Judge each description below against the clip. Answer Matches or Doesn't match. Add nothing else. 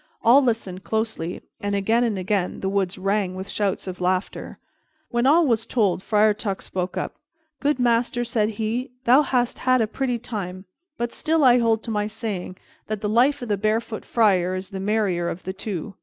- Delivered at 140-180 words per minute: Doesn't match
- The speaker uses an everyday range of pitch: Matches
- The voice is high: Matches